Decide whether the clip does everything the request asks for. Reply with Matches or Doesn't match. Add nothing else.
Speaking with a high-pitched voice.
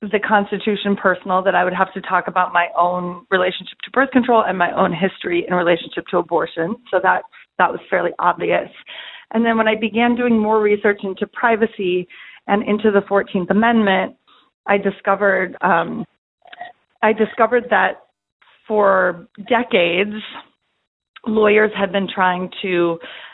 Matches